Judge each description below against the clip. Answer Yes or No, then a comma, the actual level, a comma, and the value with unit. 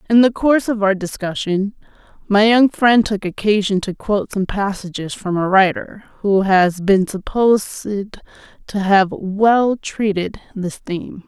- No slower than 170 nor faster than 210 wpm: No, average, 150 wpm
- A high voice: Yes, high, 205 Hz